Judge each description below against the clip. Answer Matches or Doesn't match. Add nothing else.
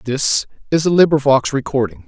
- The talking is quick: Doesn't match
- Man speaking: Matches